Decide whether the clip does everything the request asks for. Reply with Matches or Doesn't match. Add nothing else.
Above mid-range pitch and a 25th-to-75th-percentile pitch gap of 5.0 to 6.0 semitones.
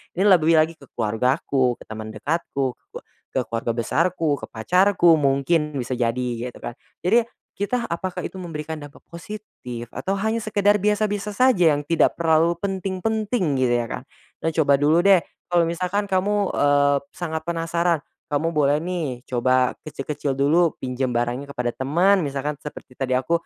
Doesn't match